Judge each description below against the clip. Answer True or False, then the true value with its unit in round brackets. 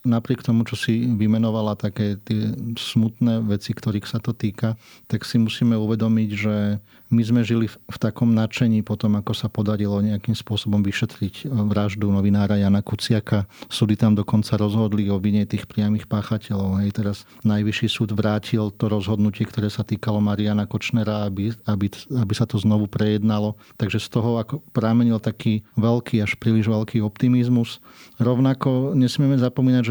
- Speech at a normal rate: True (155 wpm)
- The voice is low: True (110 Hz)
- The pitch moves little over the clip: True (1.8 semitones)